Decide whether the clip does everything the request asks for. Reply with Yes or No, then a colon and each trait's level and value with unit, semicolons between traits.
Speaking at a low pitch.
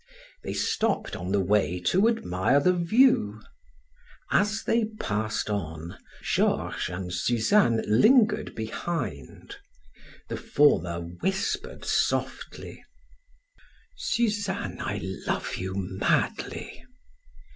Yes: low, 110 Hz